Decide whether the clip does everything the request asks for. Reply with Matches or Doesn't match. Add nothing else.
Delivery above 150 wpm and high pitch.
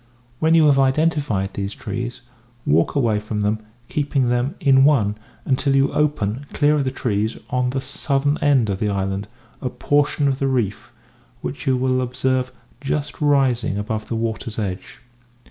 Doesn't match